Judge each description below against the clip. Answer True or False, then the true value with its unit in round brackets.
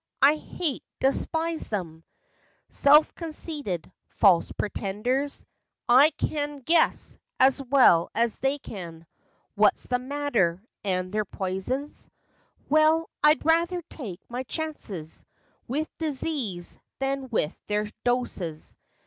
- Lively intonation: True (7.4 semitones)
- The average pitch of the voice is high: True (260 Hz)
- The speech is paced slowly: True (115 wpm)